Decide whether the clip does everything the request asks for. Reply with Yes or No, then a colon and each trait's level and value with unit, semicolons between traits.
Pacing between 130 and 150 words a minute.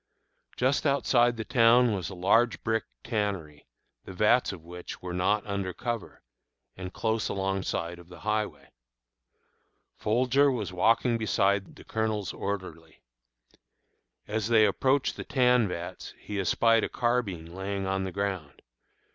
Yes: average, 140 wpm